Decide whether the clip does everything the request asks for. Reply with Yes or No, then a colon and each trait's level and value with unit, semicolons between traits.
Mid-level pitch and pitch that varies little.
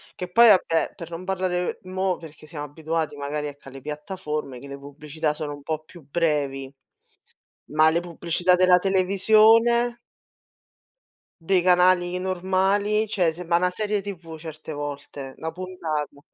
No: medium, 170 Hz; average, 3.8 semitones